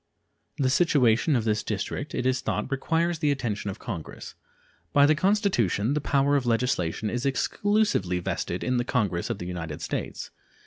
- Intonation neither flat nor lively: No, wide, 6.0 semitones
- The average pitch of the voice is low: Yes, low, 125 Hz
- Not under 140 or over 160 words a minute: No, average, 170 wpm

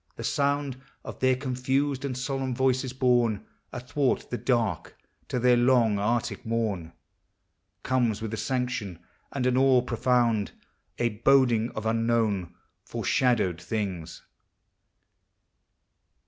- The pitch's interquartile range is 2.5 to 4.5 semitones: Yes, average, 2.9 semitones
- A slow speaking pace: Yes, slow, 115 wpm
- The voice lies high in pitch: No, low, 120 Hz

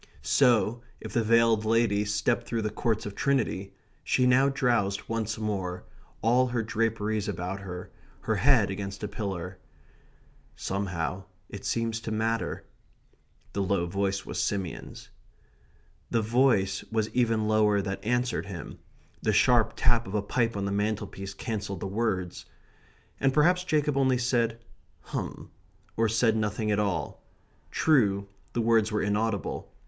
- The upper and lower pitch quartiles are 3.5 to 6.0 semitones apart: No, average, 2.8 semitones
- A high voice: No, low, 110 Hz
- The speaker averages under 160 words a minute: Yes, average, 145 wpm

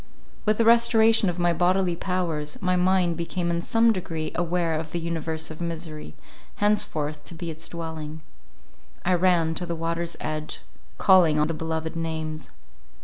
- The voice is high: No, medium, 170 Hz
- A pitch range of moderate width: No, narrow, 2.3 semitones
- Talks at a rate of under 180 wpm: Yes, average, 160 wpm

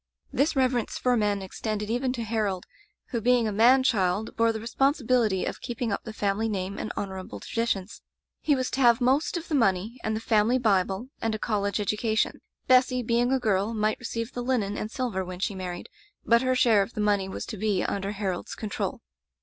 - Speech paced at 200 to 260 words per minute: Yes, fast, 205 wpm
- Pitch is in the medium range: No, high, 220 Hz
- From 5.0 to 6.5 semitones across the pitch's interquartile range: No, average, 3.4 semitones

